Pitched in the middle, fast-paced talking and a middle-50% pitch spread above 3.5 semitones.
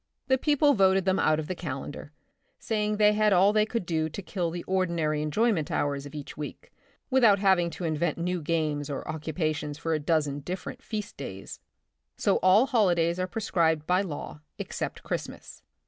No: medium, 170 Hz; average, 180 wpm; average, 4.6 semitones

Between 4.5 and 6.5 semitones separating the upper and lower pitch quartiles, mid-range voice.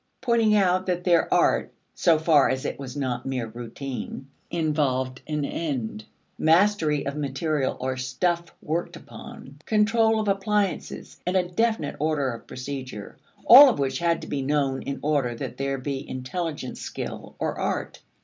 Yes: average, 5.2 semitones; medium, 150 Hz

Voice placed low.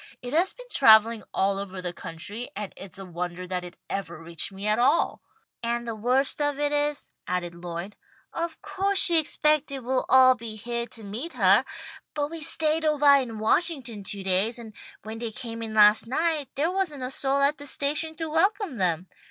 No: high, 240 Hz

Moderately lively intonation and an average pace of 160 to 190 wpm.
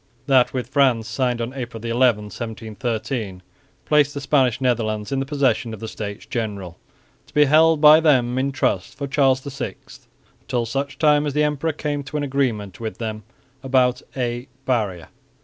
Yes: average, 3.9 semitones; average, 170 wpm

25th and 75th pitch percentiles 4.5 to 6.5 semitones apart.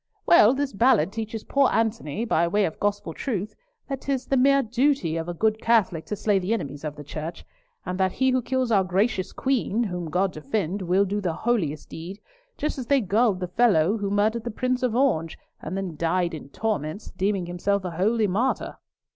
Yes: average, 5.0 semitones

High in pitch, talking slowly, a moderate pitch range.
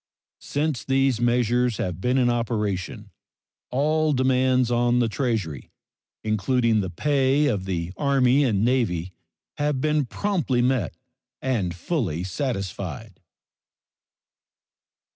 No: low, 120 Hz; slow, 105 wpm; average, 5.0 semitones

